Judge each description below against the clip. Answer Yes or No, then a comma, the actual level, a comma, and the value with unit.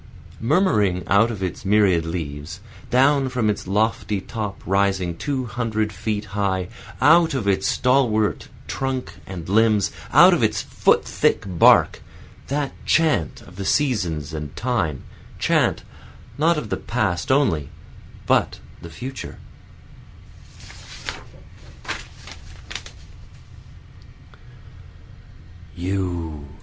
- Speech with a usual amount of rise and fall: No, wide, 5.7 semitones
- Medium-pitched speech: No, low, 105 Hz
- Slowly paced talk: Yes, slow, 100 wpm